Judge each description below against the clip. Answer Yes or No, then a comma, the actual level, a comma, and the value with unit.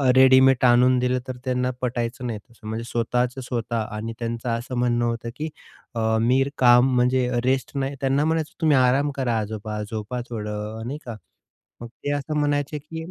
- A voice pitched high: No, low, 125 Hz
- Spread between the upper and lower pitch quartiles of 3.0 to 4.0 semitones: No, narrow, 2.4 semitones